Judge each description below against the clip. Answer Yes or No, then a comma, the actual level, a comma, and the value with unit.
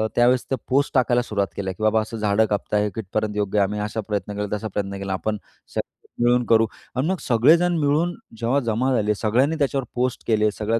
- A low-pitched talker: Yes, low, 110 Hz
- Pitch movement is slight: No, average, 3.5 semitones